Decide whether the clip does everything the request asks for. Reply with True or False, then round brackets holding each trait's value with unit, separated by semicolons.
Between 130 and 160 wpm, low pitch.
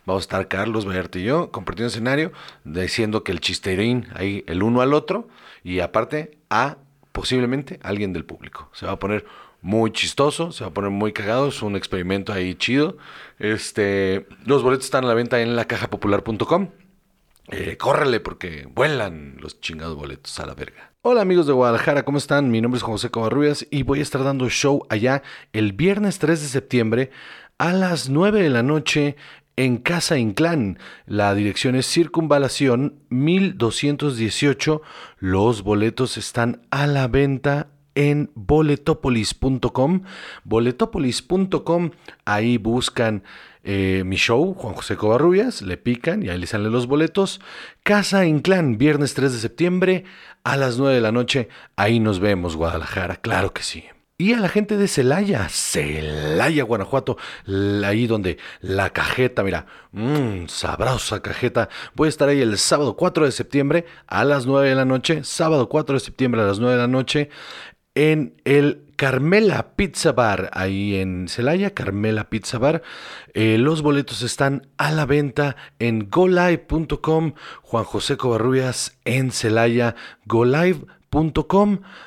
True (155 wpm; 125 Hz)